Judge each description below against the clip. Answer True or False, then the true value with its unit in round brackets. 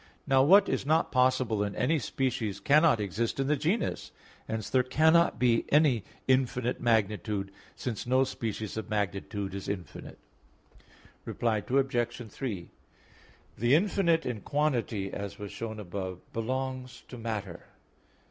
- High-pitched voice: False (120 Hz)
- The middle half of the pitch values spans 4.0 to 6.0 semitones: True (4.3 semitones)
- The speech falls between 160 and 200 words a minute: False (135 wpm)